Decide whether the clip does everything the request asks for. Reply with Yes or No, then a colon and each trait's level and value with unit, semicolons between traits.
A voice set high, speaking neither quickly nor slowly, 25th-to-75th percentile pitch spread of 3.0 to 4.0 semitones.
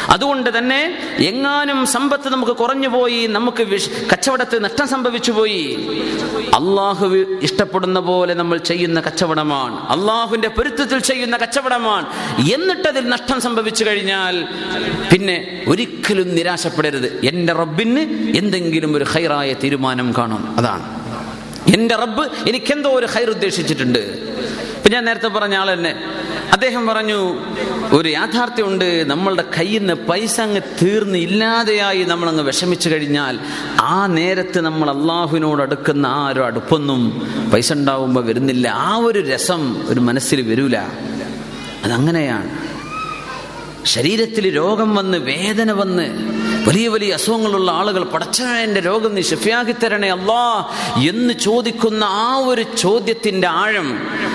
No: high, 200 Hz; average, 110 wpm; wide, 5.4 semitones